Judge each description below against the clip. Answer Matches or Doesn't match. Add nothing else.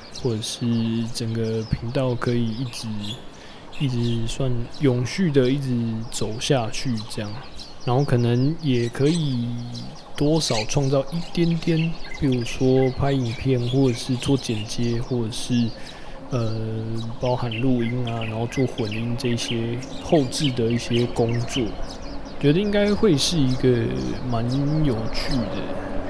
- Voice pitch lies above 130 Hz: Doesn't match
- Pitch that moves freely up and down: Doesn't match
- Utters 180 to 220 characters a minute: Matches